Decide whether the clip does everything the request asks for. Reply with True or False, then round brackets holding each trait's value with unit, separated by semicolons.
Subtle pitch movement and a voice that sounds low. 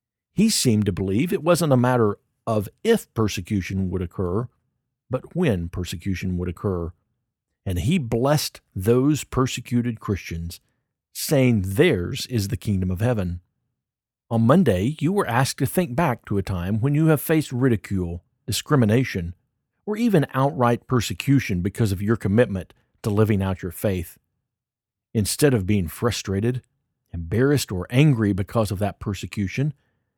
False (4.7 semitones; 115 Hz)